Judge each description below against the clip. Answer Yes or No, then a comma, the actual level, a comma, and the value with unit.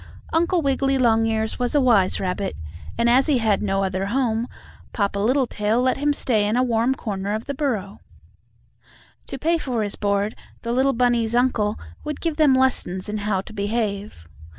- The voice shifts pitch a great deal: No, average, 4.2 semitones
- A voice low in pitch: No, high, 230 Hz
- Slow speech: No, average, 175 wpm